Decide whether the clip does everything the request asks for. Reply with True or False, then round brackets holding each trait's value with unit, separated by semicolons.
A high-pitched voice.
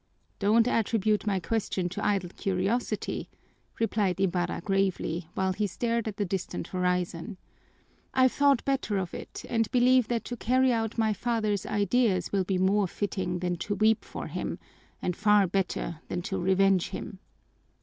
True (200 Hz)